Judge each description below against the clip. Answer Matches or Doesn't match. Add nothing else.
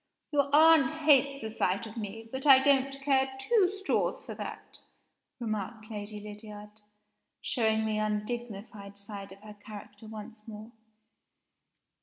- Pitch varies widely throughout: Doesn't match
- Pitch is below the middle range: Doesn't match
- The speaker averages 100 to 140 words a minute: Matches